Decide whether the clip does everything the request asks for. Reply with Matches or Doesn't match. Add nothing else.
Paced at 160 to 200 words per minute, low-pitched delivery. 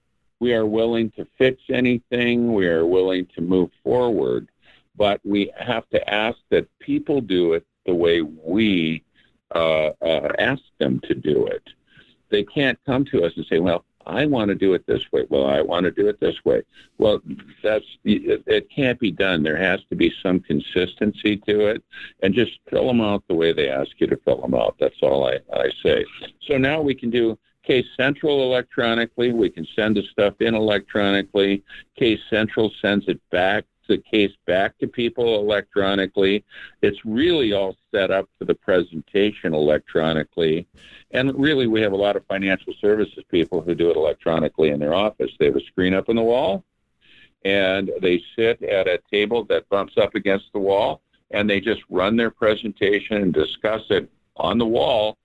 Matches